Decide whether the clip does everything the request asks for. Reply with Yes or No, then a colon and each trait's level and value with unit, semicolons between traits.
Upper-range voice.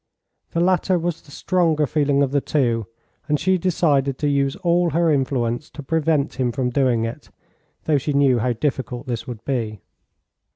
No: medium, 140 Hz